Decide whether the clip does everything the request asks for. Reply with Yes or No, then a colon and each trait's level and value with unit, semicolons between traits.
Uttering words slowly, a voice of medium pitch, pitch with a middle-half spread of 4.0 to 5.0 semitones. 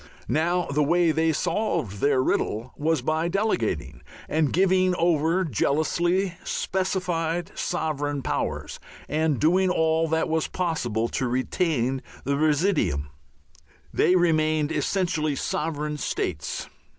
No: slow, 115 wpm; medium, 160 Hz; average, 3.5 semitones